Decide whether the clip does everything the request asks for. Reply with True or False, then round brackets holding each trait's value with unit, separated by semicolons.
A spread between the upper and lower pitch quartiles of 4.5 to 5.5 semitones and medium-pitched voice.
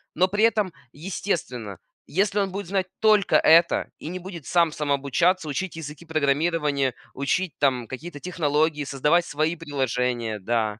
True (4.8 semitones; 155 Hz)